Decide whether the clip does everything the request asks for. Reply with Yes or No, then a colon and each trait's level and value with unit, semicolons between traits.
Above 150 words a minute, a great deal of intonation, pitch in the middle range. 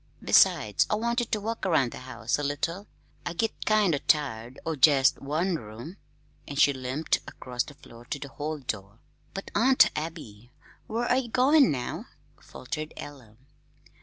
Yes: average, 165 wpm; wide, 7.8 semitones; medium, 150 Hz